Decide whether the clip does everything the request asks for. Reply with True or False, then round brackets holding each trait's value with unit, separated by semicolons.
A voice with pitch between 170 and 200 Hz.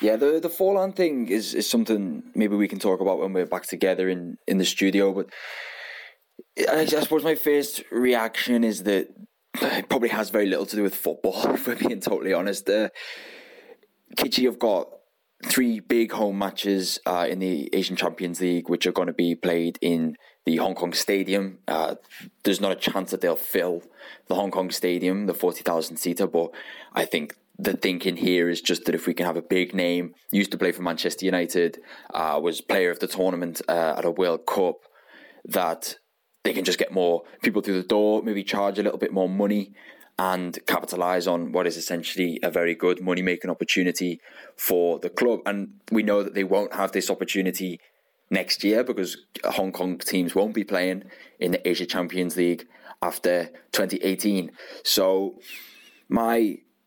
False (95 Hz)